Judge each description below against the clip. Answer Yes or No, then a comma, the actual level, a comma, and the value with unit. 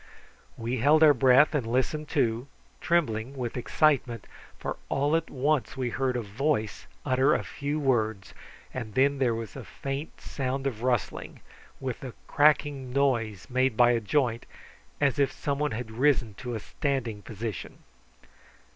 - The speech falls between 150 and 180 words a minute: Yes, average, 155 wpm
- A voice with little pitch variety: No, average, 3.4 semitones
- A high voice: No, low, 130 Hz